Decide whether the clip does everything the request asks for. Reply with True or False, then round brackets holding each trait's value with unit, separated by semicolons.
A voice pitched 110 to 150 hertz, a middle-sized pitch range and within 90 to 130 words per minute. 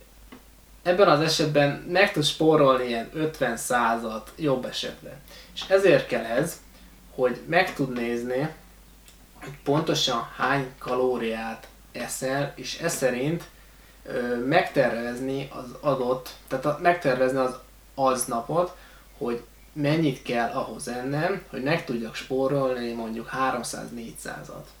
True (135 Hz; 3.9 semitones; 115 wpm)